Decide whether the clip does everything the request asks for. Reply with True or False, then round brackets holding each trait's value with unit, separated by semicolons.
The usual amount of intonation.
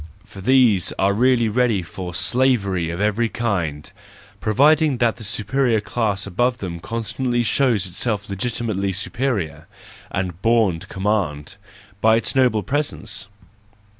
True (4.2 semitones)